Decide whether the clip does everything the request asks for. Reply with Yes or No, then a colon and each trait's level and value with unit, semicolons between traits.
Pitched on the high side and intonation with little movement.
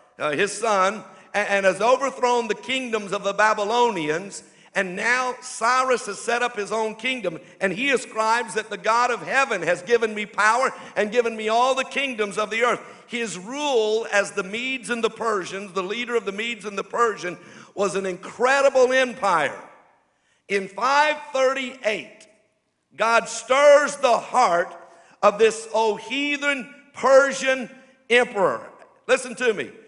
No: high, 225 Hz; average, 3.8 semitones